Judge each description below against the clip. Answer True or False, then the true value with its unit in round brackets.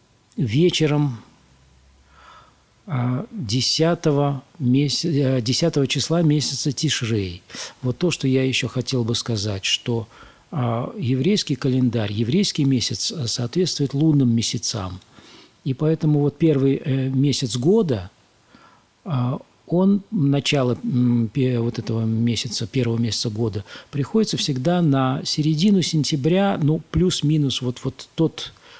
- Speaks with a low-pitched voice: True (130 Hz)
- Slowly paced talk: True (95 wpm)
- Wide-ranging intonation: False (4.5 semitones)